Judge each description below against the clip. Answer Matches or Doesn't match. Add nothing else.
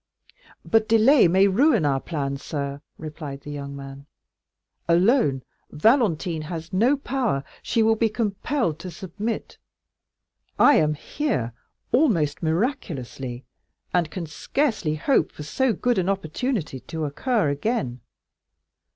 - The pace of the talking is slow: Matches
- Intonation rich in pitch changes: Matches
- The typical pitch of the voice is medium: Matches